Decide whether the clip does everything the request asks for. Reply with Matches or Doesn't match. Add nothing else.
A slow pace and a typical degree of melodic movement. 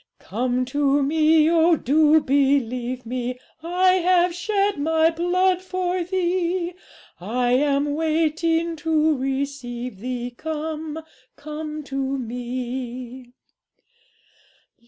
Matches